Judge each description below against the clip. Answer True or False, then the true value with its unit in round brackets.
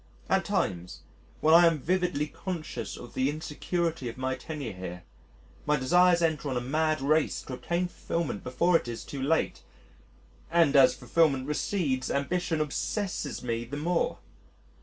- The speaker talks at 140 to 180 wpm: True (155 wpm)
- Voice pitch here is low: False (150 Hz)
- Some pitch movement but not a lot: True (4.5 semitones)